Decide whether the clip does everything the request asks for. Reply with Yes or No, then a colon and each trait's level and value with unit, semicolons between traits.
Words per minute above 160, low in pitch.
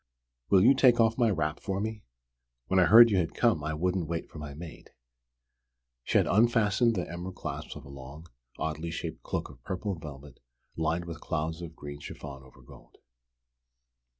Yes: average, 180 wpm; very low, 85 Hz